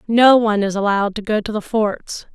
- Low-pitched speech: No, high, 210 Hz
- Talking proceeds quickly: Yes, fast, 230 wpm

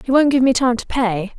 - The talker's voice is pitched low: No, high, 245 Hz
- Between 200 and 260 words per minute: No, fast, 300 wpm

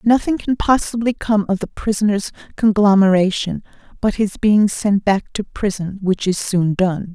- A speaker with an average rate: Yes, average, 160 wpm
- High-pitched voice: Yes, high, 200 Hz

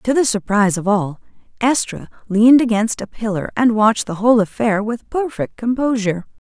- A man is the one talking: No, female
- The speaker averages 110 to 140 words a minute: No, average, 165 wpm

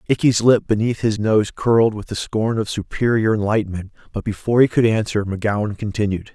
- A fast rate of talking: No, average, 180 wpm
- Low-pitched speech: Yes, low, 110 Hz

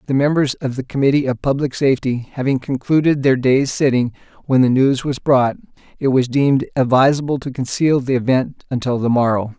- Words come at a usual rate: Yes, average, 180 wpm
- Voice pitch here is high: No, low, 130 Hz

